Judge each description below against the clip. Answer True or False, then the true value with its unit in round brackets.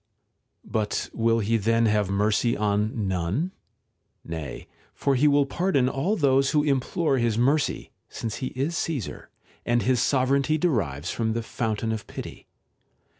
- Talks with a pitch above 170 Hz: False (120 Hz)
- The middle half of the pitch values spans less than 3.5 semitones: False (4.5 semitones)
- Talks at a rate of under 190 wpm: True (150 wpm)